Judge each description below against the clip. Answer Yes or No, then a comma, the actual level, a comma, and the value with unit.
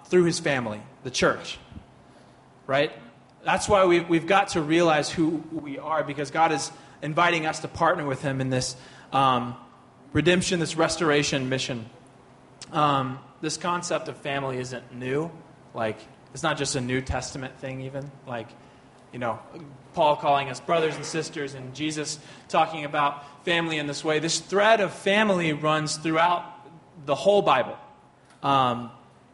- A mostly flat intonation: No, average, 3.3 semitones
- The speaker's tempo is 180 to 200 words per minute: No, average, 155 wpm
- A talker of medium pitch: Yes, medium, 150 Hz